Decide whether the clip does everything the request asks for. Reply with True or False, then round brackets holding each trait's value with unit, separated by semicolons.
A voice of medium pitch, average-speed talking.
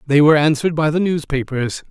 True (150 Hz; 190 wpm)